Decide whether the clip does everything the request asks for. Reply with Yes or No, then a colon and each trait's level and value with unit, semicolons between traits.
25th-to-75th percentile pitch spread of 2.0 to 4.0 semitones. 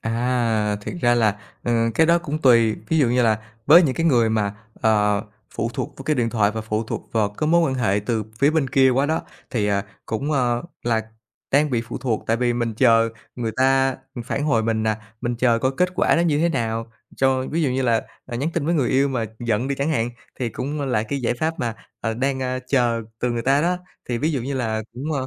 Yes: average, 3.5 semitones